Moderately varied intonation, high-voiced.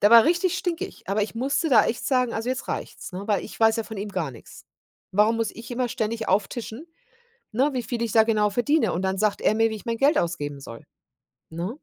Yes: average, 3.5 semitones; high, 225 Hz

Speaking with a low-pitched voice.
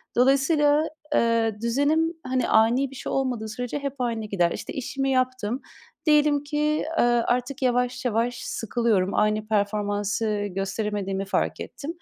No: high, 245 Hz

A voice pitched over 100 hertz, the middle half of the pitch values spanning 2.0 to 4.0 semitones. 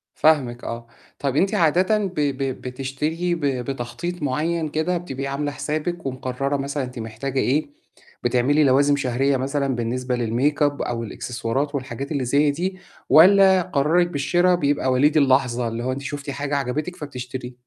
Yes: medium, 140 Hz; average, 3.2 semitones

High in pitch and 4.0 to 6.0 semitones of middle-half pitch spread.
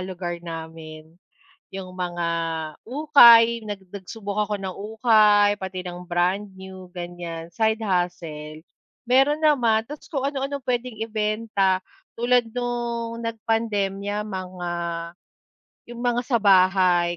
Yes: high, 205 Hz; average, 4.6 semitones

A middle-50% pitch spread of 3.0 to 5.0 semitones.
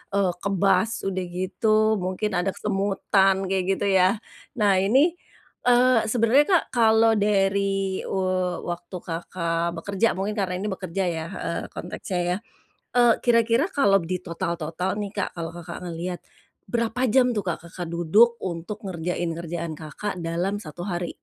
Yes: average, 3.5 semitones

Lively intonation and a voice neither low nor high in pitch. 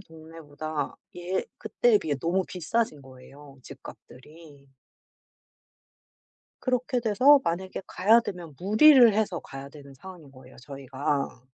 Yes: wide, 6.5 semitones; medium, 165 Hz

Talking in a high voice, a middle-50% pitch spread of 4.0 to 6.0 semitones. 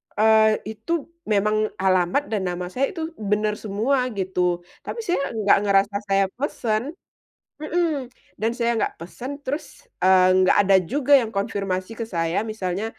Yes: high, 215 Hz; average, 5.2 semitones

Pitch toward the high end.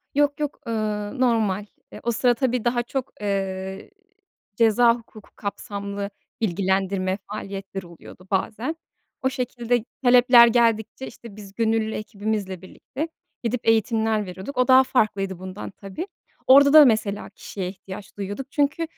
Yes: high, 220 Hz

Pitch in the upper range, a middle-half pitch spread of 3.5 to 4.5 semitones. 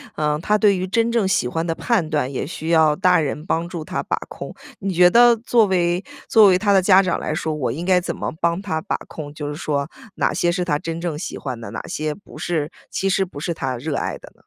No: medium, 170 Hz; average, 3.9 semitones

